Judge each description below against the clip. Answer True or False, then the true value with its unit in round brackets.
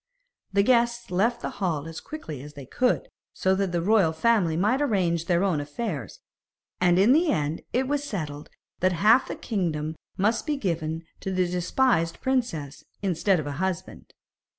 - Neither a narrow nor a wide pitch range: False (6.3 semitones)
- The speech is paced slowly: False (175 wpm)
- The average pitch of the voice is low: False (185 Hz)